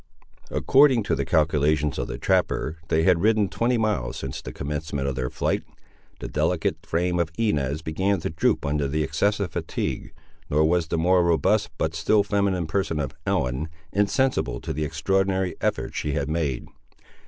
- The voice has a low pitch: Yes, very low, 80 Hz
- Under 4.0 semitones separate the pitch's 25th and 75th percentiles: No, average, 4.6 semitones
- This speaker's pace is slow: No, average, 170 wpm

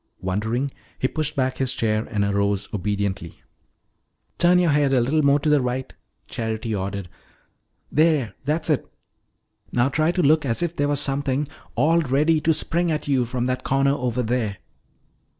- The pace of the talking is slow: No, average, 170 wpm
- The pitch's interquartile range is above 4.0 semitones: Yes, average, 5.0 semitones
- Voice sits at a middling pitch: No, low, 130 Hz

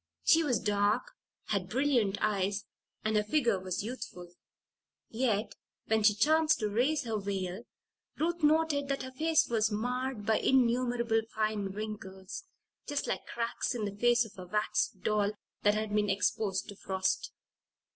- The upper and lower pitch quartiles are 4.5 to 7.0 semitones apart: No, average, 3.9 semitones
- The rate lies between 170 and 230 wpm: No, average, 155 wpm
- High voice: Yes, high, 215 Hz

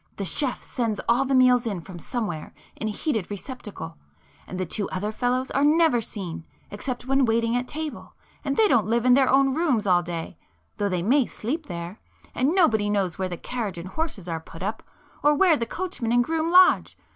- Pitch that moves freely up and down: Yes, wide, 6.3 semitones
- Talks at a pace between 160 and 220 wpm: Yes, average, 200 wpm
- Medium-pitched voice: No, high, 230 Hz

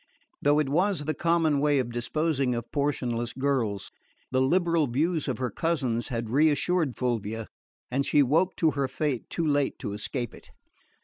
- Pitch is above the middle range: No, medium, 140 Hz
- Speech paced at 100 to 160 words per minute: No, average, 170 wpm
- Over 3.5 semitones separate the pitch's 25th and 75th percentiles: Yes, average, 4.3 semitones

